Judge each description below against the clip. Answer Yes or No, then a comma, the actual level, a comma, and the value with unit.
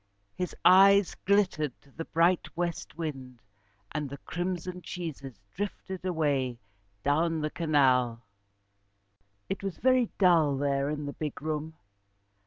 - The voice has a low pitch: No, medium, 160 Hz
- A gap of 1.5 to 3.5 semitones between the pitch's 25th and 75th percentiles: No, average, 4.3 semitones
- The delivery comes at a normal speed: No, slow, 125 wpm